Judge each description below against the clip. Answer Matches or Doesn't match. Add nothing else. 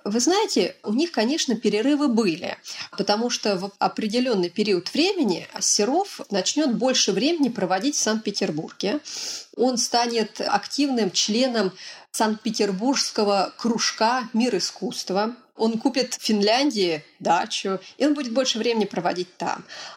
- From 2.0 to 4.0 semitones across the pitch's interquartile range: Doesn't match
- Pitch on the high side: Matches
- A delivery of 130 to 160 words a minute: Doesn't match